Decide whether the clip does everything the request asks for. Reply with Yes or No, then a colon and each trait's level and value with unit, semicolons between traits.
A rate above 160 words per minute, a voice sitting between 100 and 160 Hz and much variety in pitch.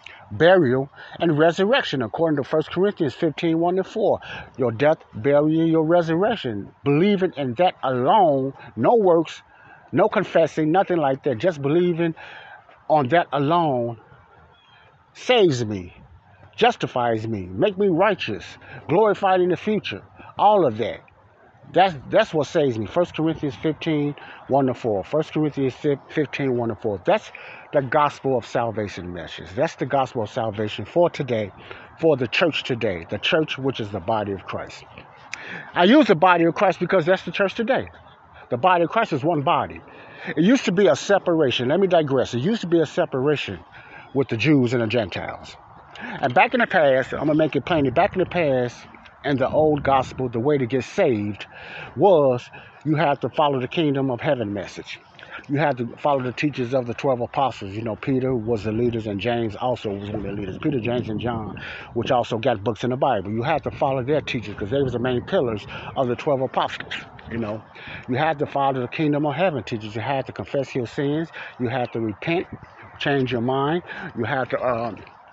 Yes: average, 190 wpm; medium, 140 Hz; wide, 5.7 semitones